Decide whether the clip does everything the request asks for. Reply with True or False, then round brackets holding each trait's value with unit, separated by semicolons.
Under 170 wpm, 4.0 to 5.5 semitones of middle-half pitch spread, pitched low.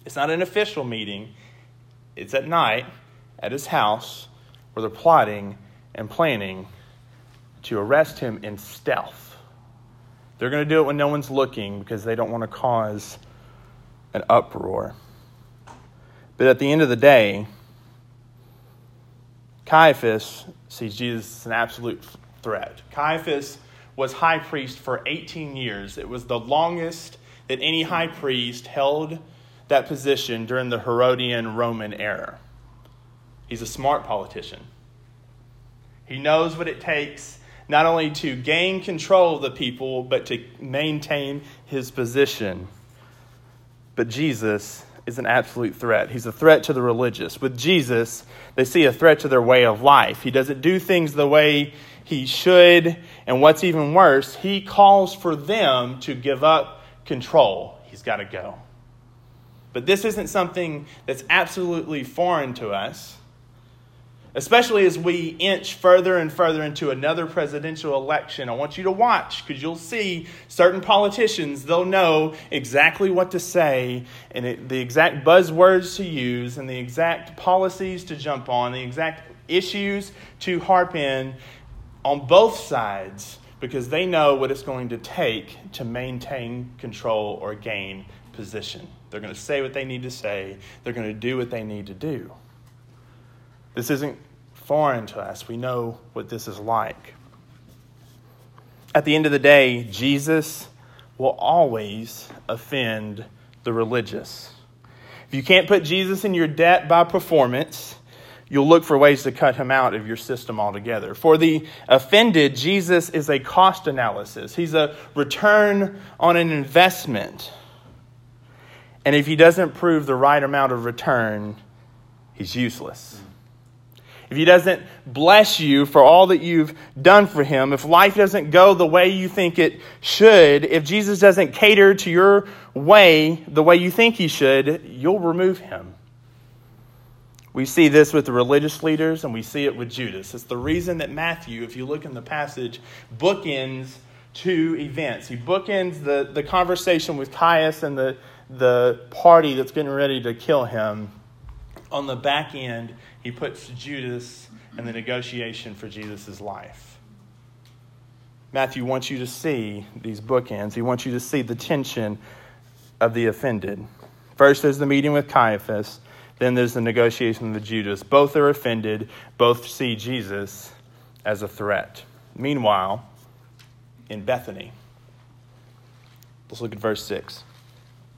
True (150 wpm; 4.3 semitones; 130 Hz)